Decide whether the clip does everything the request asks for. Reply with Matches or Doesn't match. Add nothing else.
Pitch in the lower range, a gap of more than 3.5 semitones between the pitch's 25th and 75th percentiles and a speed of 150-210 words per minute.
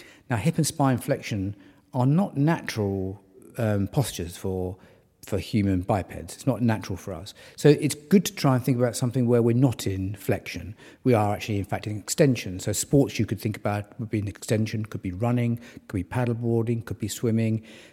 Matches